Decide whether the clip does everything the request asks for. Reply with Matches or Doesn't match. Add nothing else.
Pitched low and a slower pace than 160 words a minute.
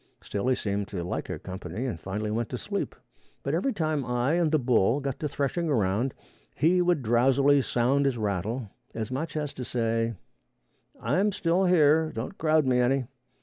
Doesn't match